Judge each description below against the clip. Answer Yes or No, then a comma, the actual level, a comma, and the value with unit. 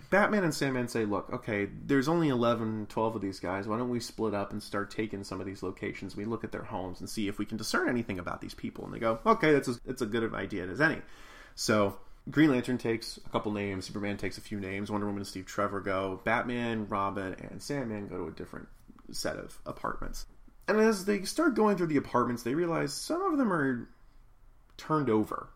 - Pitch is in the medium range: No, low, 110 Hz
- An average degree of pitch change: Yes, average, 4.6 semitones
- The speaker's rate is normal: No, fast, 230 wpm